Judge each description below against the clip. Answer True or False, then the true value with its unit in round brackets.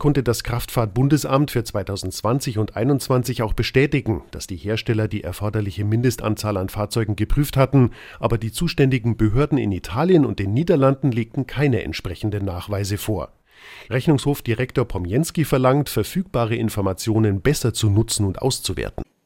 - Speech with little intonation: False (4.2 semitones)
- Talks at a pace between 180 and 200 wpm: False (135 wpm)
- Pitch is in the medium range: False (115 Hz)